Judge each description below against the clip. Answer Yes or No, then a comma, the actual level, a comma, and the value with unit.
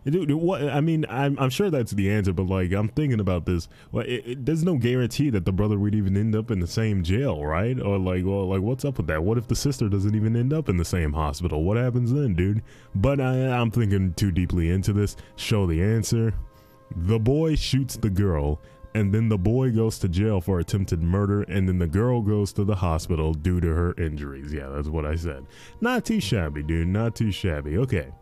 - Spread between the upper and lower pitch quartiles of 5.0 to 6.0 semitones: Yes, average, 5.3 semitones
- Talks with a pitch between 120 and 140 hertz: No, low, 105 Hz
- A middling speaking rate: No, fast, 230 wpm